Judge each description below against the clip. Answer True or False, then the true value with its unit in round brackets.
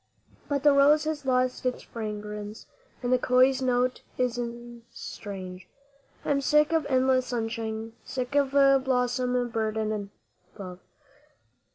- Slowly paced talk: True (125 wpm)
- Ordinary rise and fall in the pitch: True (3.5 semitones)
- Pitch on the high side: True (250 Hz)